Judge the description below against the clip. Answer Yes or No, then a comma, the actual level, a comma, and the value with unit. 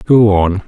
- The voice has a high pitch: No, low, 100 Hz